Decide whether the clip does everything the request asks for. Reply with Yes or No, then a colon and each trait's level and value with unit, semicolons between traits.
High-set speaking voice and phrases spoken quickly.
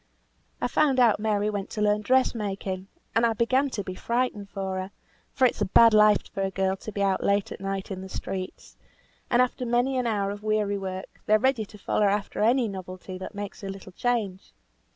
Yes: high, 205 Hz; fast, 215 wpm